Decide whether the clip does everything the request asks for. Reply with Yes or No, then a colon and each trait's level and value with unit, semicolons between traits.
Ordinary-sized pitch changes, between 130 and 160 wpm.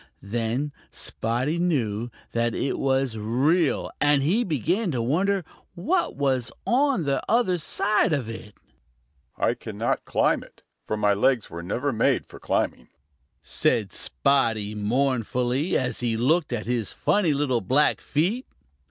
No: wide, 6.0 semitones; average, 140 wpm